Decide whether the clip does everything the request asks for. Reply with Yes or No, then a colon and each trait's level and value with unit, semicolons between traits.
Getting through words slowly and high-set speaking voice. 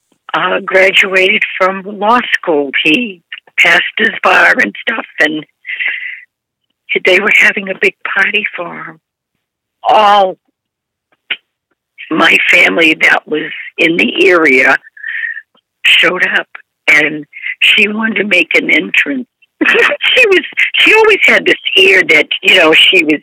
Yes: slow, 125 wpm; high, 210 Hz